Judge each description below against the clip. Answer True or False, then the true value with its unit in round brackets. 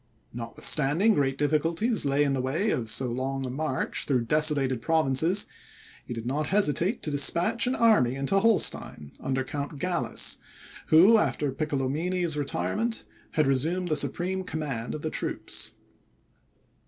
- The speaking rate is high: False (140 wpm)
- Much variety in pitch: False (4.8 semitones)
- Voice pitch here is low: False (150 Hz)